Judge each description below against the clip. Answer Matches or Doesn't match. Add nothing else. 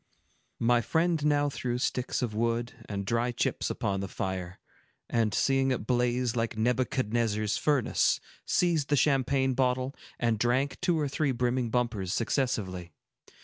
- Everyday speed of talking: Matches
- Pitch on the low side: Matches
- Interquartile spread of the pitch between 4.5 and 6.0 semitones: Doesn't match